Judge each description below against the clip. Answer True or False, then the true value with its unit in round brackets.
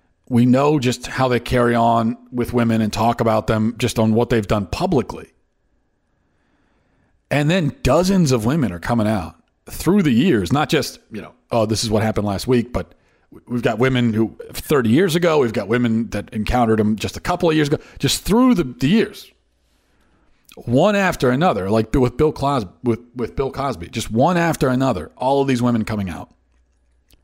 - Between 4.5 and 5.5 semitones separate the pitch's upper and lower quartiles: False (3.4 semitones)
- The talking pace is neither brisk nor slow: True (190 wpm)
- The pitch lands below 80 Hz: False (120 Hz)